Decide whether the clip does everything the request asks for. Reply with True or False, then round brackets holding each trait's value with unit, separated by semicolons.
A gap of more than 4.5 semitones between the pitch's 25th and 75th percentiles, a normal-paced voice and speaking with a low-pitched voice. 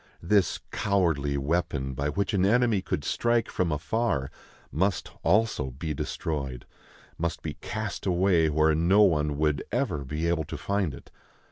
True (5.1 semitones; 150 wpm; 80 Hz)